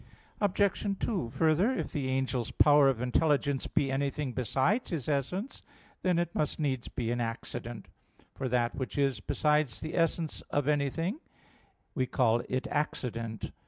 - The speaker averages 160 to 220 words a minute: No, average, 150 wpm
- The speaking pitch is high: No, medium, 140 Hz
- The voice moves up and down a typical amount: Yes, average, 4.1 semitones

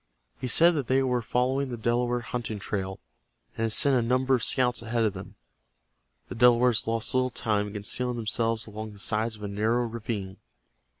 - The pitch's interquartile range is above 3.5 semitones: No, narrow, 2.5 semitones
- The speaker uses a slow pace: No, average, 190 wpm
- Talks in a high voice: No, low, 115 Hz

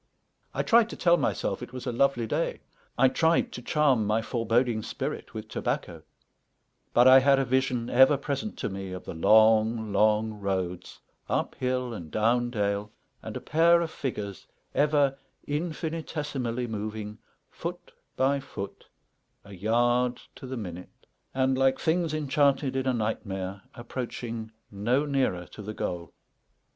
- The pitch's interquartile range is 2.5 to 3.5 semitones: No, average, 4.2 semitones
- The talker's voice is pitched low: Yes, low, 120 Hz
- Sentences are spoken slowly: No, average, 150 wpm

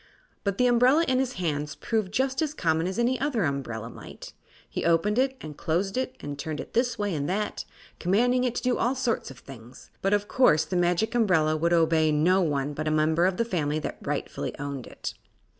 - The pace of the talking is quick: Yes, fast, 215 wpm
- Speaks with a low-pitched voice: No, medium, 180 Hz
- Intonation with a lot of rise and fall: Yes, wide, 7.7 semitones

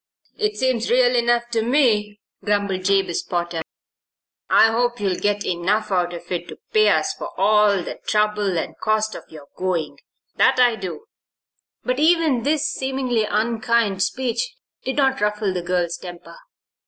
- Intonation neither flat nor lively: Yes, average, 4.7 semitones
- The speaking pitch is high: Yes, high, 215 Hz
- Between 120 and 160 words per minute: Yes, average, 155 wpm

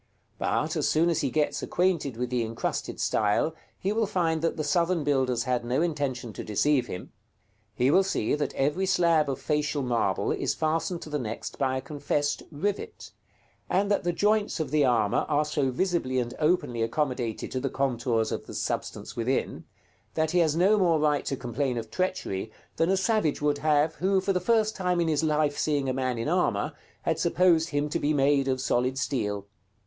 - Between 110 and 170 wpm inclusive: No, average, 200 wpm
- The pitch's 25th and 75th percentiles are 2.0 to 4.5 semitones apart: No, average, 4.9 semitones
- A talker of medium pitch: Yes, medium, 145 Hz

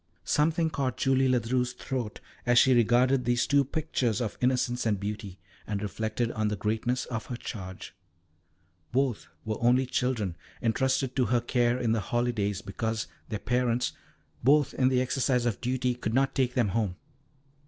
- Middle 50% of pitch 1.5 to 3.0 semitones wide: Yes, narrow, 2.5 semitones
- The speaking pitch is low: Yes, low, 120 Hz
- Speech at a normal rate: Yes, average, 165 wpm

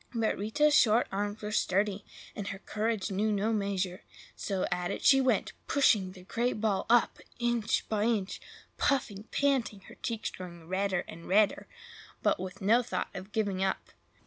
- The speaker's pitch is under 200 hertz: No, high, 205 Hz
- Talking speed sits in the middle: Yes, average, 170 wpm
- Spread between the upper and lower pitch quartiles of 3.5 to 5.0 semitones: No, average, 2.9 semitones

